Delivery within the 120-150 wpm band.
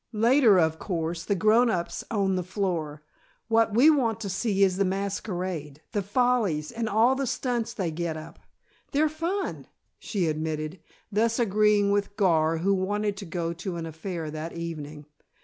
No: average, 165 wpm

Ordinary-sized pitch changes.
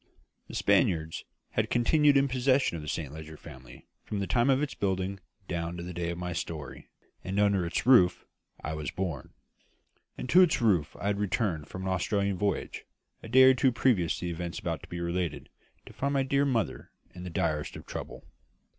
No: wide, 6.2 semitones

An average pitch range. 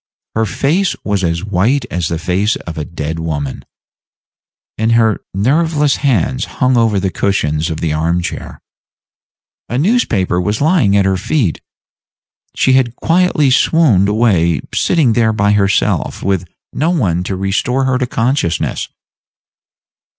No: wide, 6.6 semitones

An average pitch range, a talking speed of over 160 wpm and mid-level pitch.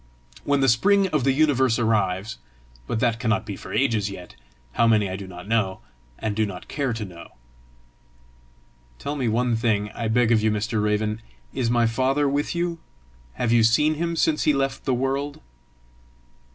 No: average, 4.3 semitones; average, 180 wpm; low, 115 Hz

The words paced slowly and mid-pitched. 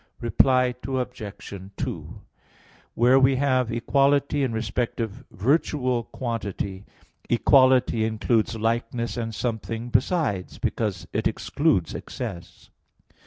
No: slow, 100 wpm; low, 120 Hz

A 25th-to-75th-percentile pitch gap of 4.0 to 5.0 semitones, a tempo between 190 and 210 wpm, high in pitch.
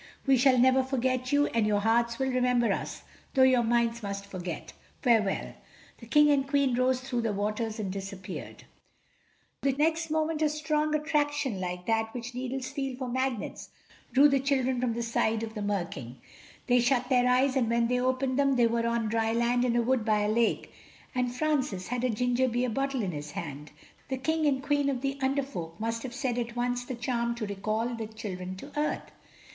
No: average, 3.1 semitones; average, 200 wpm; high, 245 Hz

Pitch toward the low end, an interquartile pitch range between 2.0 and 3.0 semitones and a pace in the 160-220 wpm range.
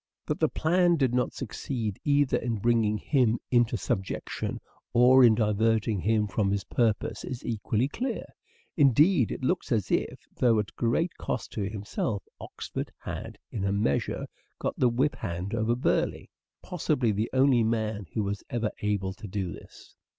No: low, 115 Hz; average, 3.6 semitones; average, 165 wpm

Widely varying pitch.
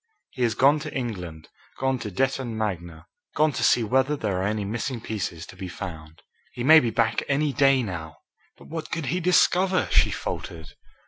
Yes: wide, 6.7 semitones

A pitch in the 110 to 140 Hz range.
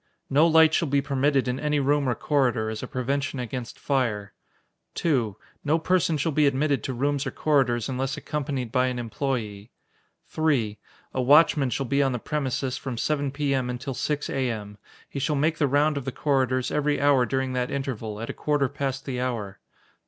Yes: low, 135 Hz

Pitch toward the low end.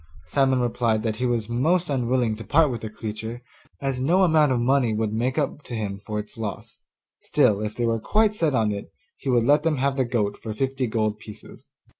Yes: low, 120 Hz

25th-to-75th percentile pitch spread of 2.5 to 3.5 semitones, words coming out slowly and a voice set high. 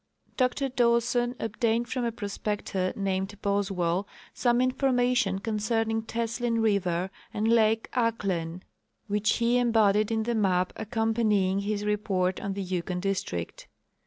Yes: average, 3.1 semitones; slow, 125 wpm; high, 215 Hz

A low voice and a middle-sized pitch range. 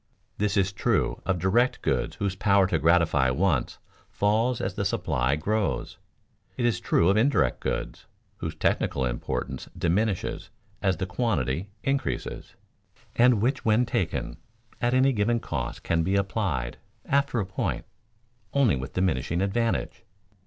No: low, 100 Hz; wide, 5.7 semitones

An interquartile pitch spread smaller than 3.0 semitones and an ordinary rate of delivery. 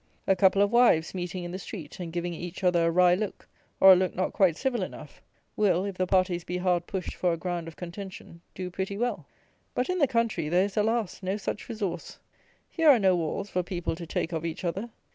No: narrow, 2.5 semitones; fast, 230 wpm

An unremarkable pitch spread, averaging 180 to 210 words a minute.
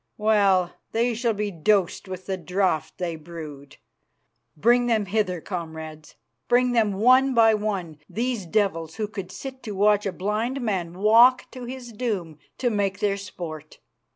No: average, 4.5 semitones; average, 155 wpm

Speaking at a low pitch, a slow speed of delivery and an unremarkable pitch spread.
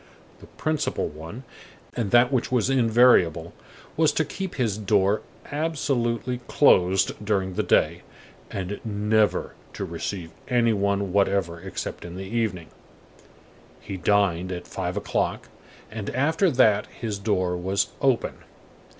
Yes: low, 105 Hz; slow, 130 wpm; average, 4.6 semitones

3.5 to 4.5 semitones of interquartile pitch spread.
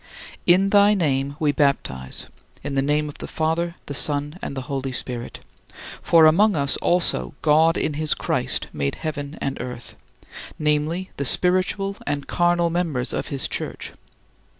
Yes: average, 3.8 semitones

